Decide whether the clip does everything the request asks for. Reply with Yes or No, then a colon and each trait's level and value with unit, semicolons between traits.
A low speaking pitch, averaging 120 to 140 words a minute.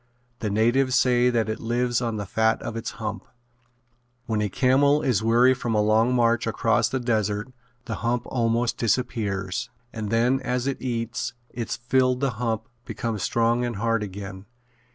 No: low, 115 Hz; average, 170 wpm